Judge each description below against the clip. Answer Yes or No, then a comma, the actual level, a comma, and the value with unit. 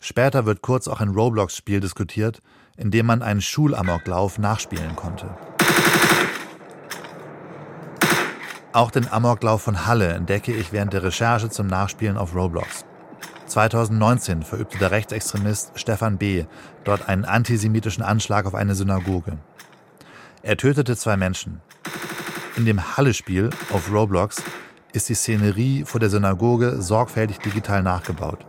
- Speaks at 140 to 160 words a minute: No, slow, 125 wpm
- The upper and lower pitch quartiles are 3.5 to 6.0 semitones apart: No, average, 2.8 semitones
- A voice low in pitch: Yes, low, 105 Hz